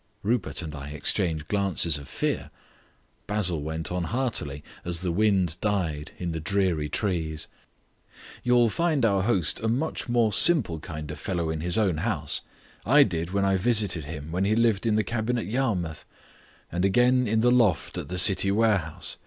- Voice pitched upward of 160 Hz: No, very low, 95 Hz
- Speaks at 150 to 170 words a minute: No, average, 180 wpm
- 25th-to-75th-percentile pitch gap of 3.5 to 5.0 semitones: No, wide, 5.6 semitones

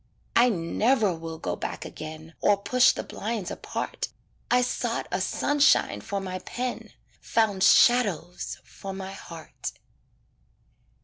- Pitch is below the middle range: No, high, 195 Hz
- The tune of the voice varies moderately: No, wide, 5.8 semitones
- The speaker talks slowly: Yes, slow, 125 wpm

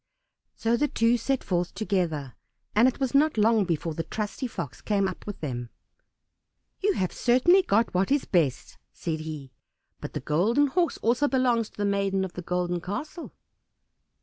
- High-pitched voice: Yes, high, 205 Hz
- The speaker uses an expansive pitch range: Yes, wide, 6.2 semitones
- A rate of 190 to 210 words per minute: No, average, 175 wpm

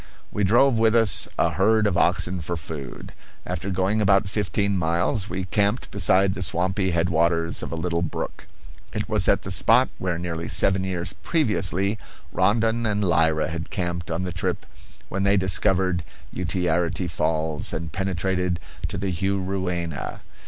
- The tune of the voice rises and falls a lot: No, average, 2.7 semitones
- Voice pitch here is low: Yes, very low, 95 Hz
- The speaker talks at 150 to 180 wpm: Yes, average, 155 wpm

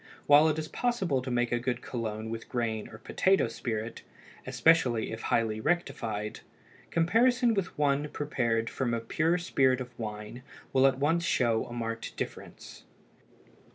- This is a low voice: Yes, low, 125 Hz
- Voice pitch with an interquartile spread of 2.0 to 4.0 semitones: No, wide, 5.5 semitones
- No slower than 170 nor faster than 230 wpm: No, average, 150 wpm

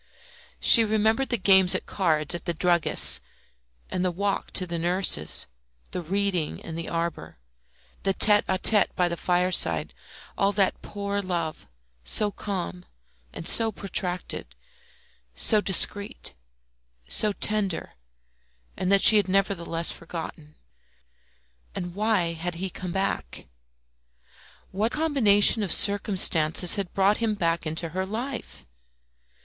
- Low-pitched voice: No, medium, 185 Hz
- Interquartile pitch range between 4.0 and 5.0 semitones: No, average, 3.1 semitones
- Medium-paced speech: No, slow, 130 wpm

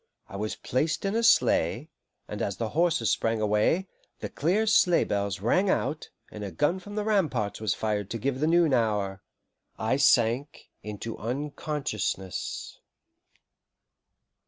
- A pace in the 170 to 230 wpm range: No, average, 145 wpm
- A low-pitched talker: Yes, low, 125 Hz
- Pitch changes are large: Yes, wide, 7.8 semitones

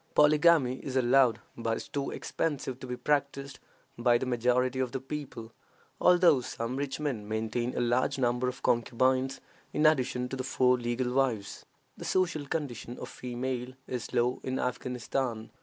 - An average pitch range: No, narrow, 2.1 semitones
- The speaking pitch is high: No, low, 130 Hz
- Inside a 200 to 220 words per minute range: No, average, 160 wpm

